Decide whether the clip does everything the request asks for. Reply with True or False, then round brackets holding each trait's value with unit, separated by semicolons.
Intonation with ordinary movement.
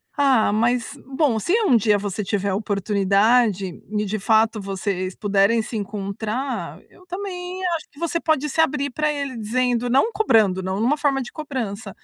False (5.8 semitones)